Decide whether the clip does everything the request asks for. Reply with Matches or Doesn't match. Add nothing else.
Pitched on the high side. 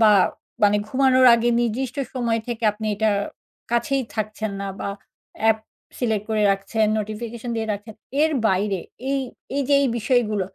Matches